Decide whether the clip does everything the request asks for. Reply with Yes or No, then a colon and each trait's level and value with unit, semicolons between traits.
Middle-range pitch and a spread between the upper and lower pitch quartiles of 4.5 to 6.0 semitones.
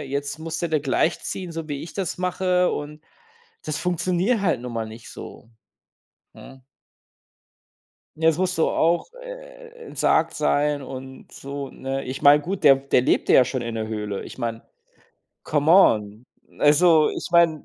Yes: medium, 150 Hz; average, 5.1 semitones